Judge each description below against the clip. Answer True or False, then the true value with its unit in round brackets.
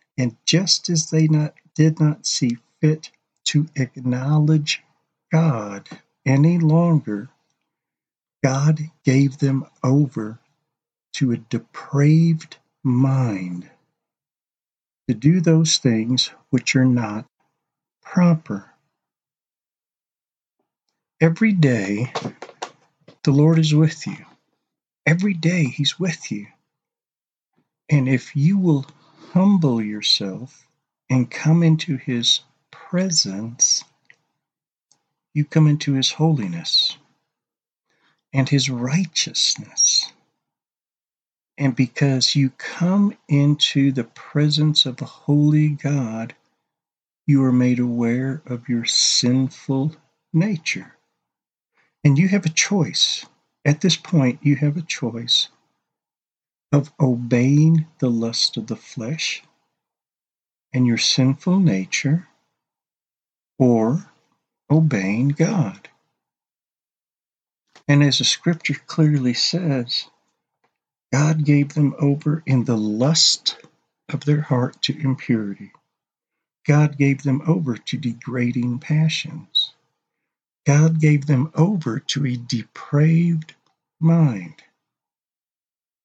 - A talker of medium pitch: True (145 Hz)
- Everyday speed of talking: False (95 wpm)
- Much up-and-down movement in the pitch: False (3.9 semitones)